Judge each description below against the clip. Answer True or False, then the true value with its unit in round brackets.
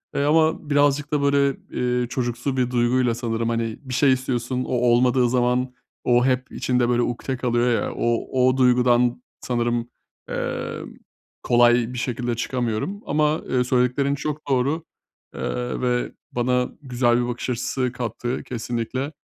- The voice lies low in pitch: True (125 Hz)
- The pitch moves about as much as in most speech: False (1.5 semitones)